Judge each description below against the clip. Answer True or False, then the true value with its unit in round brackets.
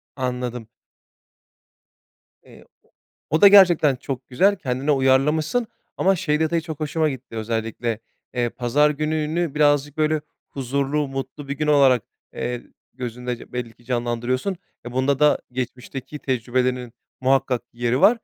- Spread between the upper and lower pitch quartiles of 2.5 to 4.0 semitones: True (3.5 semitones)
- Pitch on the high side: False (135 Hz)